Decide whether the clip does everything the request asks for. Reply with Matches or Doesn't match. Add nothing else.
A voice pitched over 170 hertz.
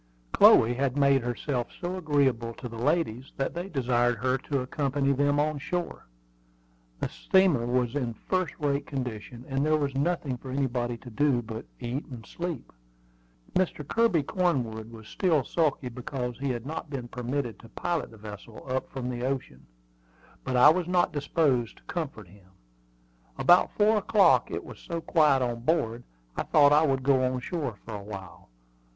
Doesn't match